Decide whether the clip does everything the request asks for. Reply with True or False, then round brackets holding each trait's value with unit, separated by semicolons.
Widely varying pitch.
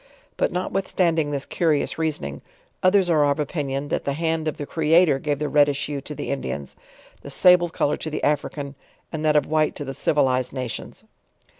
False (2.4 semitones)